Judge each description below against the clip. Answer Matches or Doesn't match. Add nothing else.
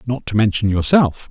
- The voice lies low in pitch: Matches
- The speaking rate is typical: Matches